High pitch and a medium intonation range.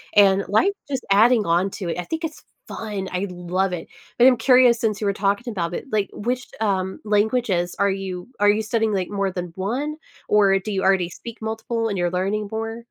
Yes: high, 205 Hz; average, 3.0 semitones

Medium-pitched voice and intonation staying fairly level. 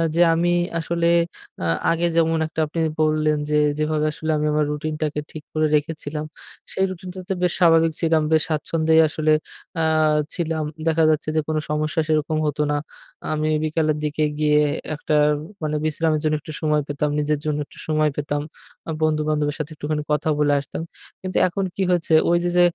Yes: medium, 155 Hz; narrow, 1.3 semitones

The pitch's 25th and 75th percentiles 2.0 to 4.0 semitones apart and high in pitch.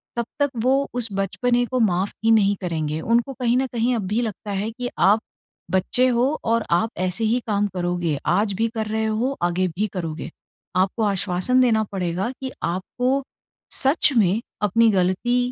No: average, 4.7 semitones; high, 215 Hz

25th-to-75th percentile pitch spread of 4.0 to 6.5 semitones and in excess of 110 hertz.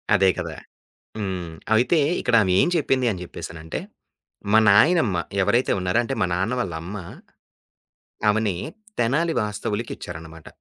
No: average, 4.8 semitones; low, 105 Hz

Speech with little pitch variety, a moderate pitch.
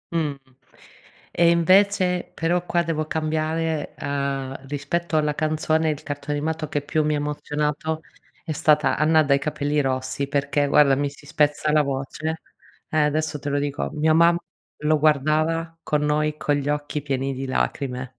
Yes: narrow, 1.8 semitones; medium, 150 Hz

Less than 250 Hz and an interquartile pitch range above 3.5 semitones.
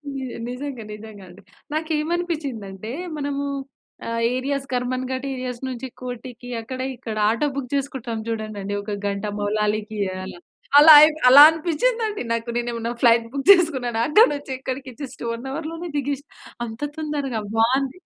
No: very high, 255 Hz; average, 4.1 semitones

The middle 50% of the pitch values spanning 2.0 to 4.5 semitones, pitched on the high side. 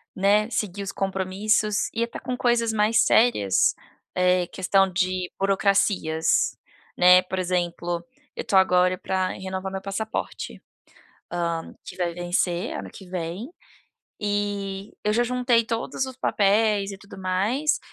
Yes: average, 2.8 semitones; high, 195 Hz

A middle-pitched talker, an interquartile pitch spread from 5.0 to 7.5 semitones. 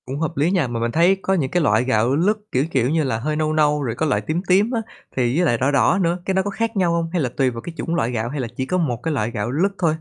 Yes: medium, 150 Hz; wide, 5.6 semitones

